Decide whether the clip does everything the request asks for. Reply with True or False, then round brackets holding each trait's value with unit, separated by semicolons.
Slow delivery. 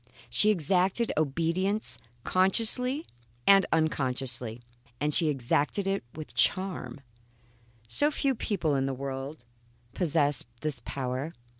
True (110 wpm)